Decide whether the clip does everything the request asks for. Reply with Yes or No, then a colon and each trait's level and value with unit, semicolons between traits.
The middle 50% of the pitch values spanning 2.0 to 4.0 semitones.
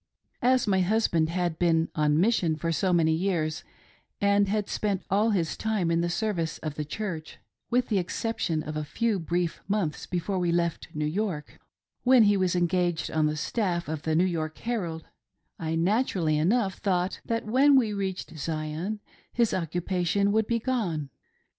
No: average, 4.5 semitones